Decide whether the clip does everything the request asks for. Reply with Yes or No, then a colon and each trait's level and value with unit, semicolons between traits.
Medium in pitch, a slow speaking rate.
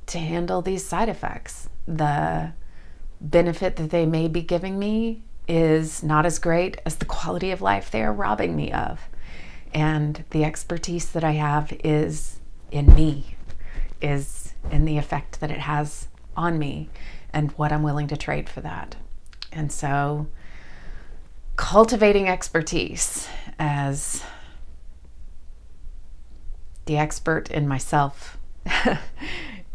Yes: medium, 150 Hz; slow, 125 wpm